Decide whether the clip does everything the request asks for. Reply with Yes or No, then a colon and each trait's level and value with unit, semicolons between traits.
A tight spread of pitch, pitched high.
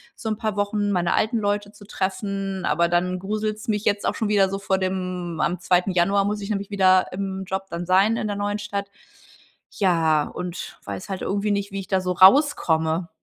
Yes: narrow, 2.1 semitones; high, 195 Hz